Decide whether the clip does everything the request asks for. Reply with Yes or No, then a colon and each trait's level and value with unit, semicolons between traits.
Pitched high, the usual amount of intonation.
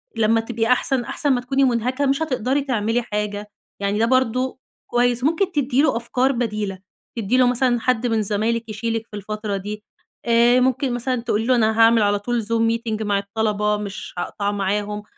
Yes: high, 230 Hz; average, 3.1 semitones